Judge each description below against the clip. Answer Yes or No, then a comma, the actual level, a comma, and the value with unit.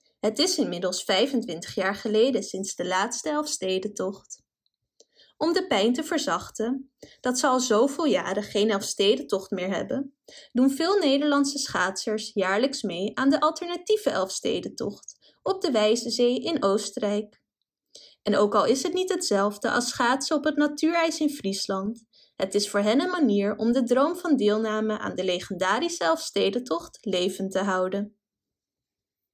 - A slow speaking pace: No, average, 145 wpm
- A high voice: Yes, high, 225 Hz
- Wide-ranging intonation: Yes, wide, 6.1 semitones